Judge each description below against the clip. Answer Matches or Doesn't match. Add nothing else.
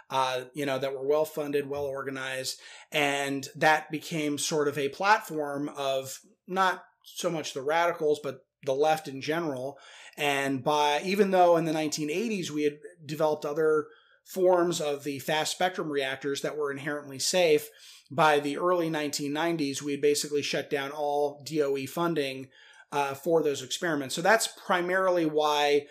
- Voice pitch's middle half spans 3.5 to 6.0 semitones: Doesn't match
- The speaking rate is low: Doesn't match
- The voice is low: Doesn't match